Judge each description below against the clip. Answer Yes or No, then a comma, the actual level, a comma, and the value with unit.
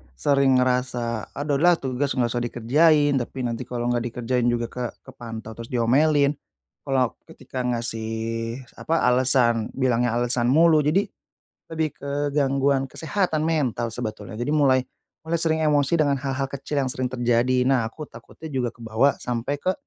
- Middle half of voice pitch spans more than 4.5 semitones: No, average, 3.3 semitones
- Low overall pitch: Yes, low, 130 Hz